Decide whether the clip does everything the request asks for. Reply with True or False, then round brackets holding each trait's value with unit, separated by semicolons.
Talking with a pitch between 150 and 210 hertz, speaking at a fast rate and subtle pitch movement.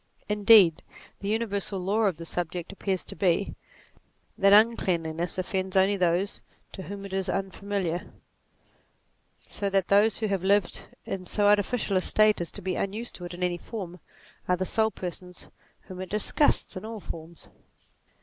False (190 Hz; 175 wpm; 2.2 semitones)